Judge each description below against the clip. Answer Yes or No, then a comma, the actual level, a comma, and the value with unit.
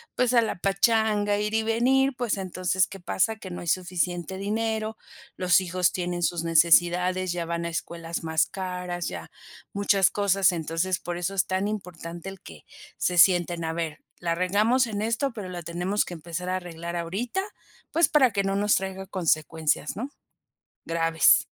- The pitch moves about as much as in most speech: Yes, average, 3.2 semitones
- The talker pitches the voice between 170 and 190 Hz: Yes, medium, 185 Hz